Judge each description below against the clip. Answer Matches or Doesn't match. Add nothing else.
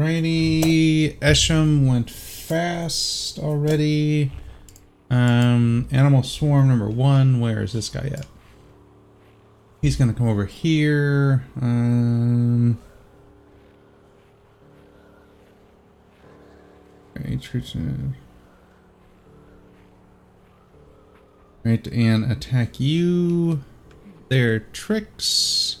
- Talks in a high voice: Doesn't match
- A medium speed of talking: Doesn't match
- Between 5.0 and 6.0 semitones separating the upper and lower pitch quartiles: Matches